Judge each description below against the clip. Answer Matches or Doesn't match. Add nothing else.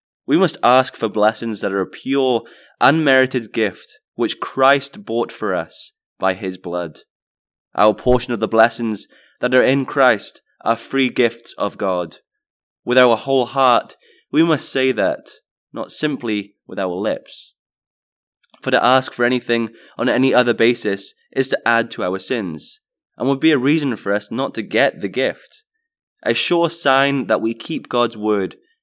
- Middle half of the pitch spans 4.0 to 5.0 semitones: Doesn't match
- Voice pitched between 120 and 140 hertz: Matches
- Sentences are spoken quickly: Doesn't match